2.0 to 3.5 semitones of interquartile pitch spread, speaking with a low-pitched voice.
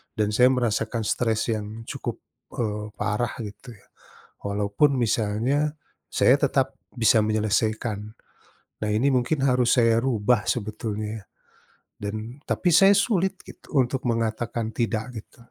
Yes: average, 2.8 semitones; low, 115 Hz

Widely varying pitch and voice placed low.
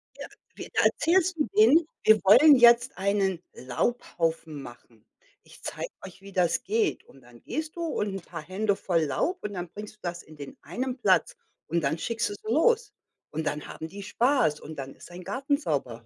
No: wide, 7.6 semitones; high, 195 Hz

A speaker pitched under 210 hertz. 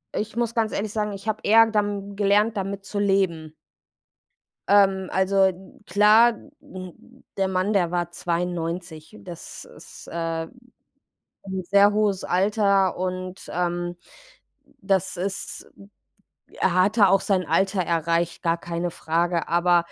Yes: high, 190 Hz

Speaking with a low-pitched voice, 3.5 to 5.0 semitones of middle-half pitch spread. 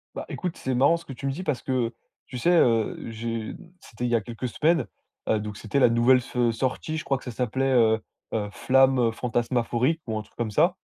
No: low, 125 Hz; average, 2.8 semitones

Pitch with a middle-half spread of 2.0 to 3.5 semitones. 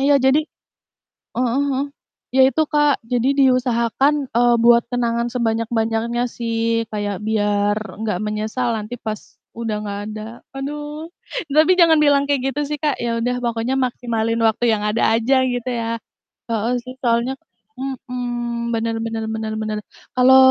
Yes: narrow, 2.6 semitones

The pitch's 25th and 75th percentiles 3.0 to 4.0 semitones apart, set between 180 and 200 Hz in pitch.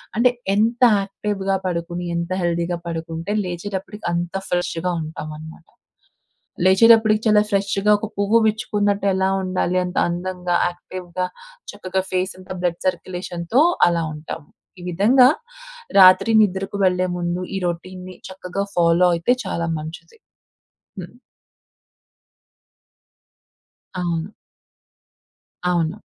No: narrow, 2.6 semitones; medium, 185 Hz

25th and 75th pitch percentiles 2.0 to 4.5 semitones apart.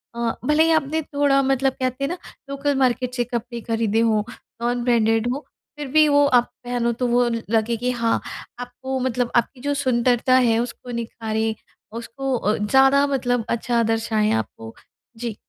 Yes: narrow, 2.6 semitones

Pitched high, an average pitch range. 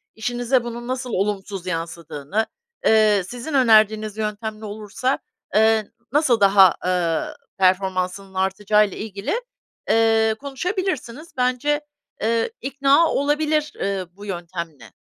Yes: high, 215 Hz; average, 4.6 semitones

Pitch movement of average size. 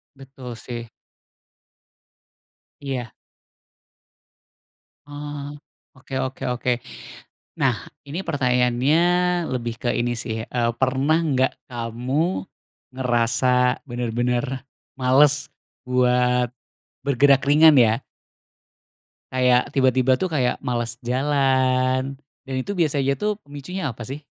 No: narrow, 2.3 semitones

